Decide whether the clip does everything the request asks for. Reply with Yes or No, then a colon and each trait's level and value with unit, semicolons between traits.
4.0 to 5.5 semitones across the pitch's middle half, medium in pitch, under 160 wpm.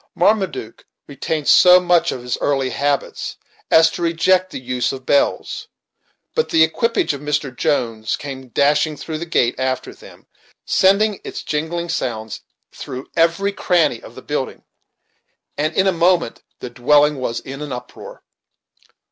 Yes: average, 4.9 semitones; medium, 150 Hz; average, 150 wpm